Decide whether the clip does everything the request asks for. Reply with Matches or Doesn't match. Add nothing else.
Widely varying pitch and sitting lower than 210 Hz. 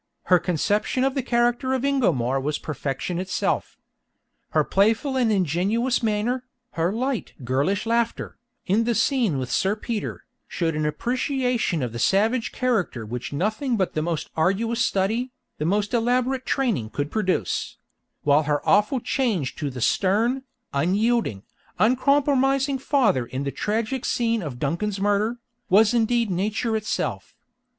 Doesn't match